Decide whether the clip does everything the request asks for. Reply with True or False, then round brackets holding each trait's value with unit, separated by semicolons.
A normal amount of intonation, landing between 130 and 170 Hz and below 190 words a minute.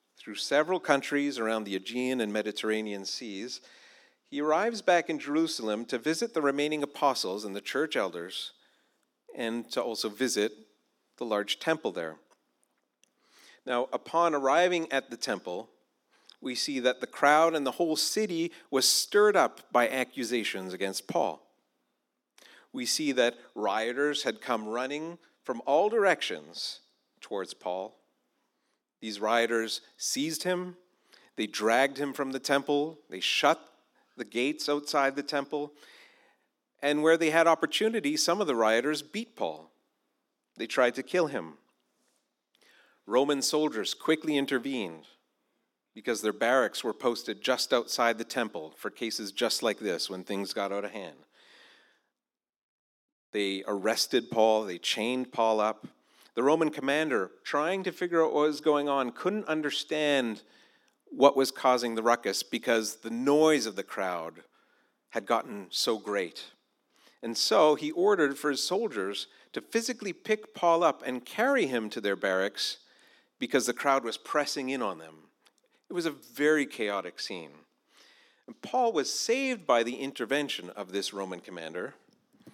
False (6.1 semitones; 140 Hz; 145 wpm)